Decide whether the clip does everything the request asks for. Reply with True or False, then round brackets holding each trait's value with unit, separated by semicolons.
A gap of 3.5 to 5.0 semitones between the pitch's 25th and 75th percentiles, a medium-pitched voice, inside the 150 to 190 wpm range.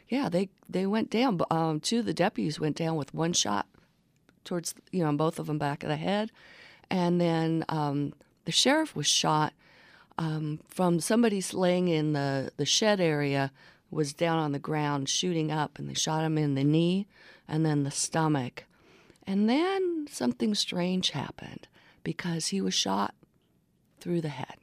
True (4.1 semitones; 165 Hz; 175 wpm)